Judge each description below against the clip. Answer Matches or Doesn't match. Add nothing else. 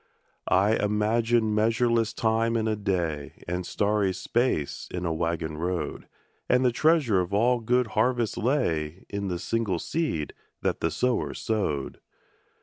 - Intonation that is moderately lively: Matches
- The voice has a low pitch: Matches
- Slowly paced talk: Doesn't match